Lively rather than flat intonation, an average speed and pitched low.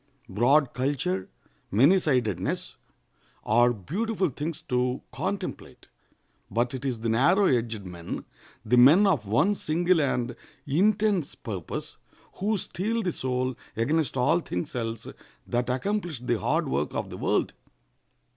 No: wide, 7.0 semitones; slow, 125 wpm; low, 130 Hz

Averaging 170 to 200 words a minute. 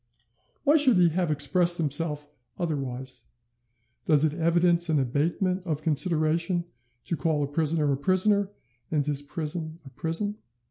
No: average, 140 wpm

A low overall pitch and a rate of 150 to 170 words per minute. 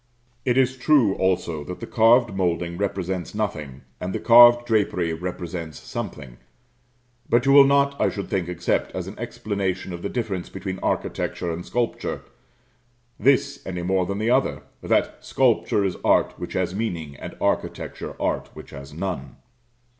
Yes: very low, 95 Hz; average, 160 wpm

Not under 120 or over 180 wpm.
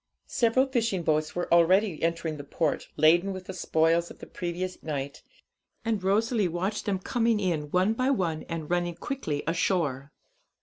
Yes: average, 165 wpm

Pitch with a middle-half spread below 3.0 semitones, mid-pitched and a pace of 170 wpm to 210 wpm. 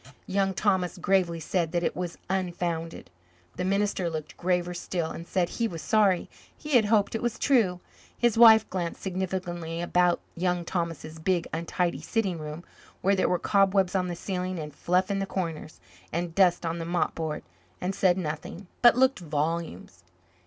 Yes: narrow, 2.4 semitones; medium, 180 Hz; average, 175 wpm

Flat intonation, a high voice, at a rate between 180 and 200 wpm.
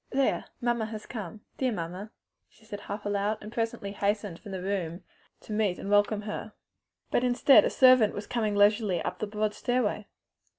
Yes: narrow, 1.9 semitones; high, 210 Hz; average, 185 wpm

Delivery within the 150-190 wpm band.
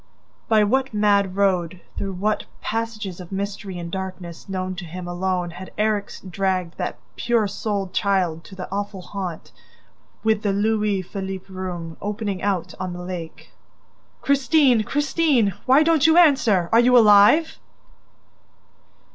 No: average, 140 wpm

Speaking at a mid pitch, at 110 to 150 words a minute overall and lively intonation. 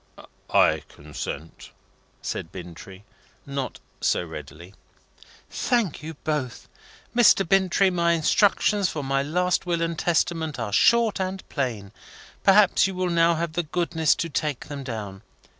Yes: medium, 160 Hz; slow, 135 wpm; wide, 6.8 semitones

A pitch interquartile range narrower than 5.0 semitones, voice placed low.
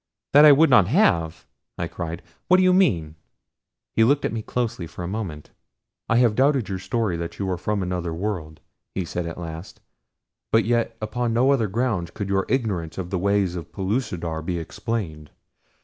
No: wide, 5.6 semitones; low, 100 Hz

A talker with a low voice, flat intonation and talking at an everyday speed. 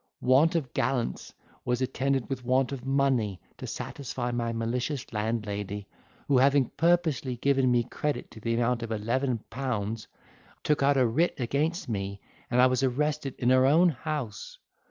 No: low, 125 Hz; average, 3.1 semitones; average, 160 wpm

